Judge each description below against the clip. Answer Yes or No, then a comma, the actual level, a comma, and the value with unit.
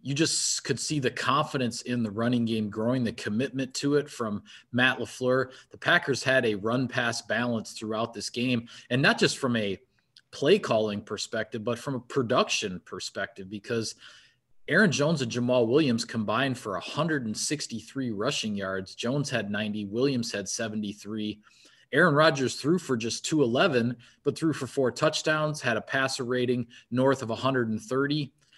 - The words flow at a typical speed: Yes, average, 160 wpm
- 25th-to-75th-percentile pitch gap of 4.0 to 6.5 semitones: No, average, 3.2 semitones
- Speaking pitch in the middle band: No, low, 125 Hz